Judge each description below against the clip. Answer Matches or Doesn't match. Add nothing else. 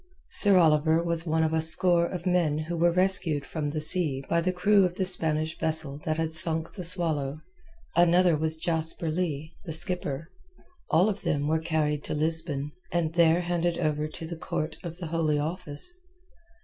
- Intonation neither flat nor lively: Doesn't match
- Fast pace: Doesn't match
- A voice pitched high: Doesn't match